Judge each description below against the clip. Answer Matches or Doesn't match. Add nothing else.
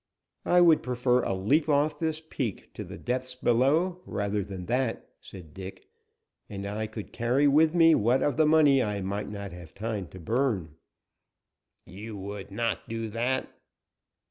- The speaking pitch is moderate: Doesn't match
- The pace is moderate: Matches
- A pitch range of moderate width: Doesn't match